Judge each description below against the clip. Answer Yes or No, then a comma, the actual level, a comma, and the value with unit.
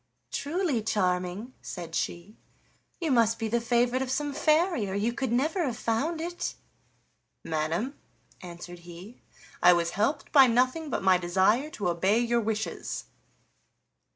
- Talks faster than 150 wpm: No, average, 145 wpm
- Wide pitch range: Yes, wide, 6.7 semitones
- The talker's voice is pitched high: Yes, high, 230 Hz